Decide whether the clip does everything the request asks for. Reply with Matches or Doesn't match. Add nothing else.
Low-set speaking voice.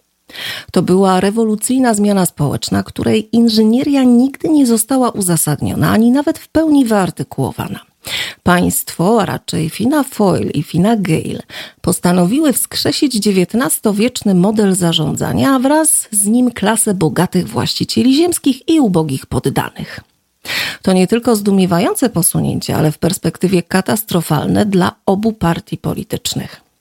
Doesn't match